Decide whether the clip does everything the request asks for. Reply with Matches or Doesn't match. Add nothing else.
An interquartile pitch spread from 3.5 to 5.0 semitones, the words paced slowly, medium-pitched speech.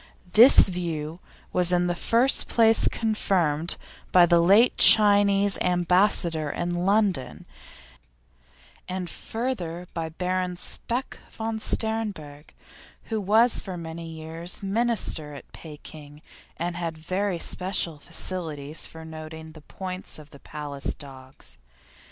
Matches